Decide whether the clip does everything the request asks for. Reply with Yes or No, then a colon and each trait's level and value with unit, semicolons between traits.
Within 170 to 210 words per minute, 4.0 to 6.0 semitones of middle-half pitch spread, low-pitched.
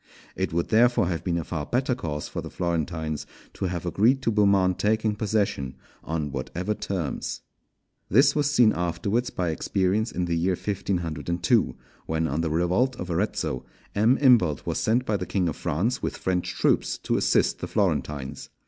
Yes: average, 175 wpm; average, 4.8 semitones; very low, 90 Hz